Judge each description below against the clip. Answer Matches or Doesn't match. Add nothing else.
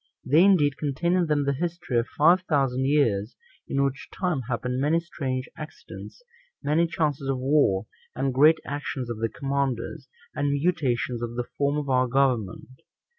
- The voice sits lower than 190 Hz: Matches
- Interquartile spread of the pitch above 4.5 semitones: Doesn't match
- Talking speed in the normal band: Matches